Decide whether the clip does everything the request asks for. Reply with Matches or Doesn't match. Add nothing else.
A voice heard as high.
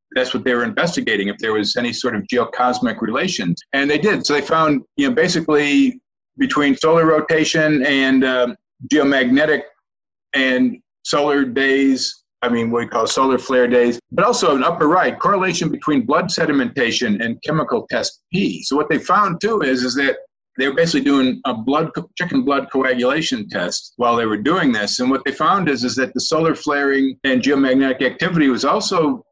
Doesn't match